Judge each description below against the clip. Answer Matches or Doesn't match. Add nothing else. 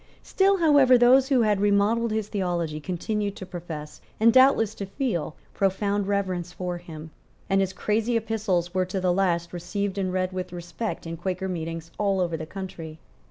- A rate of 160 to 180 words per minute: Matches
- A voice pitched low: Doesn't match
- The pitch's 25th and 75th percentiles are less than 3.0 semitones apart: Doesn't match